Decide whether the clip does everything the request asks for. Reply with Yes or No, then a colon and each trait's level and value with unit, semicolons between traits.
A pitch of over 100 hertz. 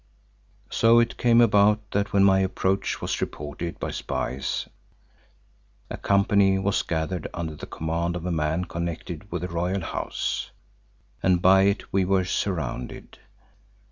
No: very low, 95 Hz